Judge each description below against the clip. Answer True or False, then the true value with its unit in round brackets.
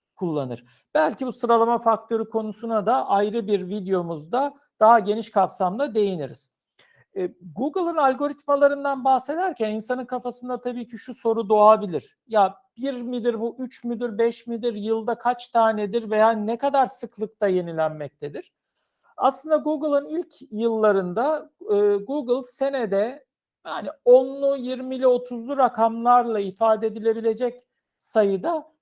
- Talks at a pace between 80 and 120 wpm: True (110 wpm)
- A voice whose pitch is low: False (235 Hz)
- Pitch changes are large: False (3.6 semitones)